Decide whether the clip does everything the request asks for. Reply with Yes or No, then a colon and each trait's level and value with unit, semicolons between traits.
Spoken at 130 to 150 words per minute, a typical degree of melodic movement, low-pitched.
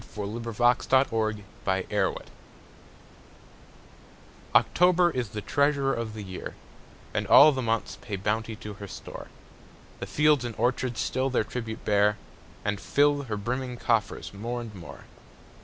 Yes: average, 140 wpm; average, 3.8 semitones; low, 115 Hz